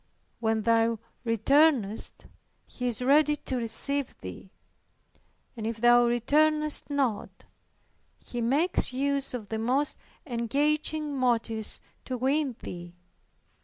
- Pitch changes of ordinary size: Yes, average, 4.0 semitones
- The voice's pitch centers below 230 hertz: No, very high, 250 Hz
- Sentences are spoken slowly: Yes, slow, 110 wpm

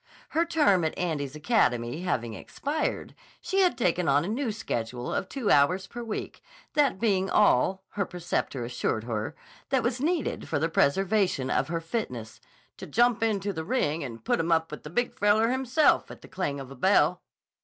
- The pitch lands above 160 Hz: Yes, medium, 185 Hz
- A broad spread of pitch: Yes, wide, 8.4 semitones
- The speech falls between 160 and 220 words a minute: Yes, average, 185 wpm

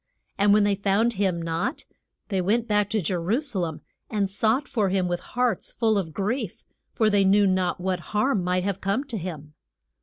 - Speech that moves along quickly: Yes, fast, 210 wpm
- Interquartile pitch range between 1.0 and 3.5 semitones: Yes, average, 3.1 semitones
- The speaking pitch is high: Yes, high, 200 Hz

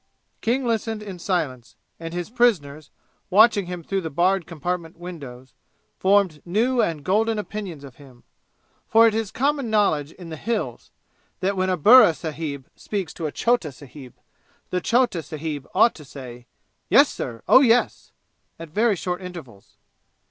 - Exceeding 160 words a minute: No, average, 155 wpm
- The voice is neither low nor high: Yes, medium, 180 Hz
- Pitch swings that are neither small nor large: No, wide, 6.1 semitones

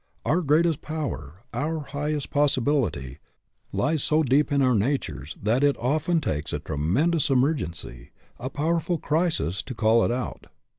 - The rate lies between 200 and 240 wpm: No, average, 150 wpm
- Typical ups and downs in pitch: No, wide, 6.0 semitones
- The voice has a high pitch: No, medium, 140 Hz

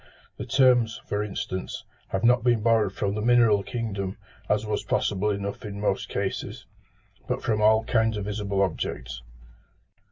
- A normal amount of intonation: No, narrow, 2.2 semitones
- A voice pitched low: Yes, low, 105 Hz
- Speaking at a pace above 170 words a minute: No, average, 155 wpm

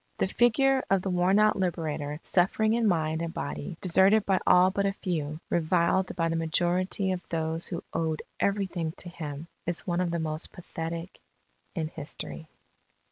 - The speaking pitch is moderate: Yes, medium, 175 Hz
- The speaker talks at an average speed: Yes, average, 170 wpm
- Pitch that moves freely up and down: No, average, 2.8 semitones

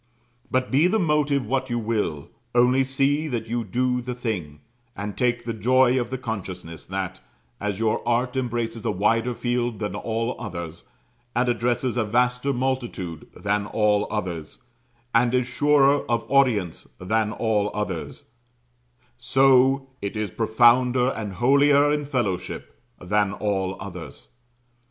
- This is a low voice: Yes, low, 120 Hz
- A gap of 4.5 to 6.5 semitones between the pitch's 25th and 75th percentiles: No, average, 3.8 semitones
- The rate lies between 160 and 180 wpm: No, average, 140 wpm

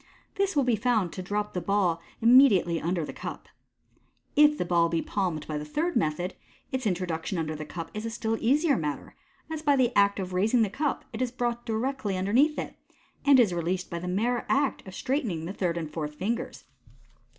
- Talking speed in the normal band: No, fast, 210 wpm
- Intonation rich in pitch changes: Yes, wide, 6.5 semitones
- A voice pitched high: Yes, high, 200 Hz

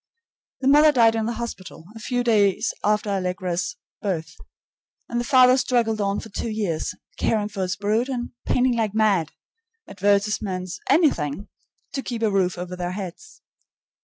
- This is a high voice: Yes, high, 210 Hz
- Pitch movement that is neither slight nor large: Yes, average, 4.2 semitones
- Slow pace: No, average, 160 wpm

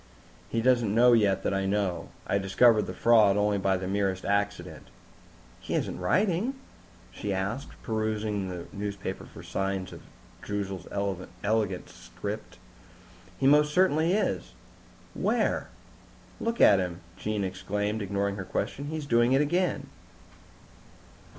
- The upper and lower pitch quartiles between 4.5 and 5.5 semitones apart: No, average, 3.9 semitones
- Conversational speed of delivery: No, slow, 130 wpm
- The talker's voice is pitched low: Yes, low, 105 Hz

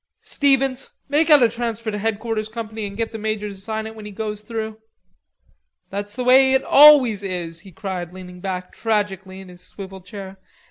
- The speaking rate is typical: Yes, average, 190 wpm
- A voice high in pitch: Yes, high, 215 Hz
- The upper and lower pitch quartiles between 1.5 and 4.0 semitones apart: Yes, average, 3.1 semitones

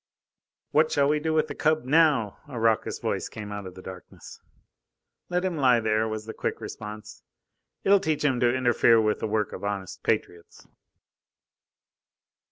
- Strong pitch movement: Yes, wide, 6.0 semitones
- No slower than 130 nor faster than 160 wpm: No, average, 170 wpm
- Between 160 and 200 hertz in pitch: No, low, 115 Hz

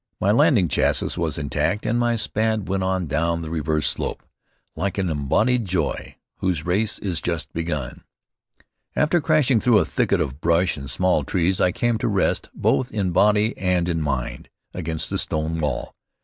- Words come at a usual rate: Yes, average, 175 wpm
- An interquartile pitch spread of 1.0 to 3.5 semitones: No, average, 5.2 semitones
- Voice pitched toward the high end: No, very low, 90 Hz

